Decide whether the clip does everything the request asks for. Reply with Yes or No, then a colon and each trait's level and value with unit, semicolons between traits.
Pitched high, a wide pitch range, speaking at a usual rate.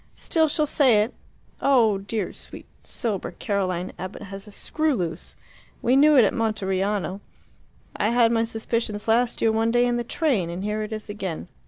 No: high, 220 Hz; average, 3.3 semitones; average, 180 wpm